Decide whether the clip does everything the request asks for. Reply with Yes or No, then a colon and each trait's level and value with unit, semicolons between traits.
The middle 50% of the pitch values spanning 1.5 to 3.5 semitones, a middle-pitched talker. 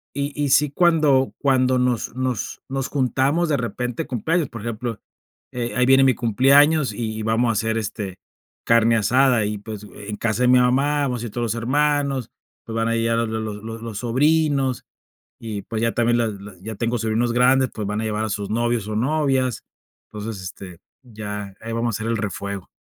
No: average, 3.2 semitones; low, 120 Hz